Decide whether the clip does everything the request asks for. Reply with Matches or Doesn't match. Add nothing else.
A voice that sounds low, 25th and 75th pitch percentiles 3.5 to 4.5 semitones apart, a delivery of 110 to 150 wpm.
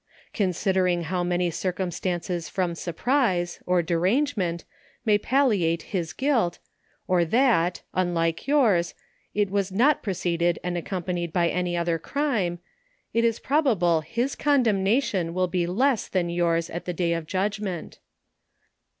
Doesn't match